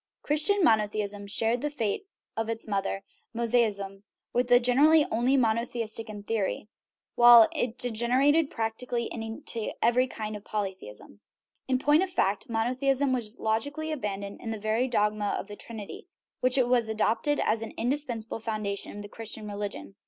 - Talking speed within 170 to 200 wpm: No, average, 155 wpm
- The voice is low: No, high, 225 Hz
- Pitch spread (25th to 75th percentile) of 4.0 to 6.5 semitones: No, average, 3.0 semitones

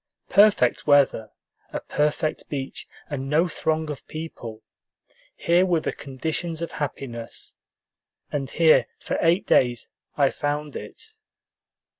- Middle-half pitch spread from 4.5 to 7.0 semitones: No, average, 3.4 semitones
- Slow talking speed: Yes, slow, 120 wpm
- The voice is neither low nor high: Yes, medium, 150 Hz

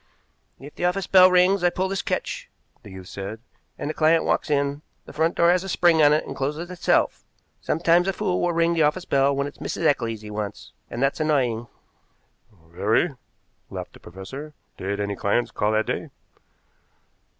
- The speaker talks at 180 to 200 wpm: Yes, average, 190 wpm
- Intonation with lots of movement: Yes, wide, 7.7 semitones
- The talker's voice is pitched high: No, medium, 150 Hz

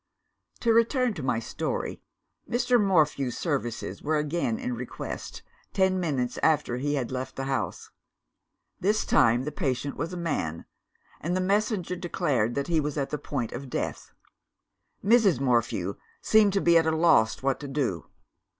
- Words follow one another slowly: No, average, 160 wpm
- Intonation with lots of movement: Yes, wide, 6.3 semitones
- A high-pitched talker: No, medium, 150 Hz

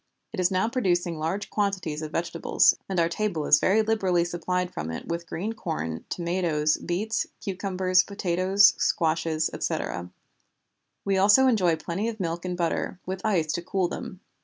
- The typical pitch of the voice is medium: Yes, medium, 180 Hz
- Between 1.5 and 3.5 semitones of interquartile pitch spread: Yes, average, 2.9 semitones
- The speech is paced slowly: No, average, 160 wpm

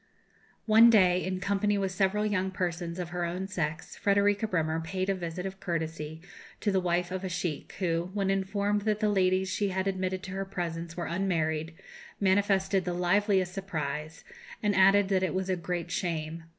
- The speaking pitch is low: No, medium, 185 Hz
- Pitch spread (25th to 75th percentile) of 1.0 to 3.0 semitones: Yes, narrow, 2.4 semitones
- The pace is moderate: Yes, average, 185 wpm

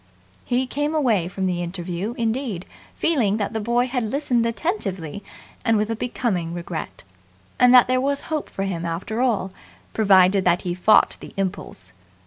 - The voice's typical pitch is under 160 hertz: No, high, 215 Hz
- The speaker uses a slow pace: No, average, 165 wpm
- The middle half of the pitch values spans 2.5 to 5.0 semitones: No, wide, 5.4 semitones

